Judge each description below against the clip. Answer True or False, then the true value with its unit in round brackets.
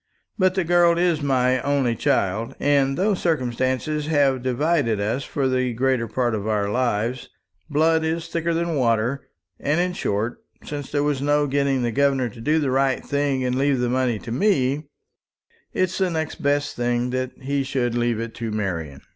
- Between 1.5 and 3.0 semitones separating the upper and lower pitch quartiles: False (3.6 semitones)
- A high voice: False (135 Hz)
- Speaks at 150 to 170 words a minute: False (180 wpm)